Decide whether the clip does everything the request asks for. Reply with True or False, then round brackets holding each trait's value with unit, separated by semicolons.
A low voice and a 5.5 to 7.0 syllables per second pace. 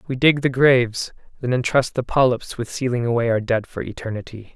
True (125 Hz; 5.6 syllables/s)